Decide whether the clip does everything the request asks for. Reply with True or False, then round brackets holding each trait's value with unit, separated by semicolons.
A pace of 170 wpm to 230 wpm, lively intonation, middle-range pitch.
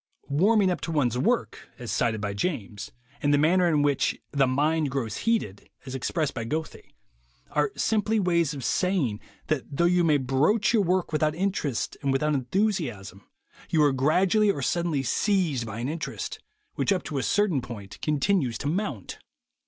True (175 wpm; 5.8 semitones; 150 Hz)